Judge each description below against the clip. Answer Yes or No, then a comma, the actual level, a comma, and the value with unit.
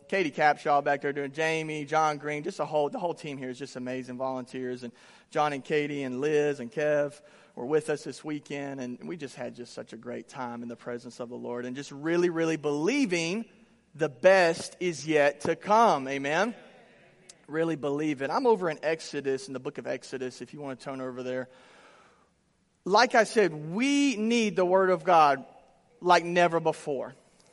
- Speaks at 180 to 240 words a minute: Yes, average, 195 wpm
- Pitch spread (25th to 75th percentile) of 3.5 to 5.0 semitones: Yes, average, 4.3 semitones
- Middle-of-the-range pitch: Yes, medium, 150 Hz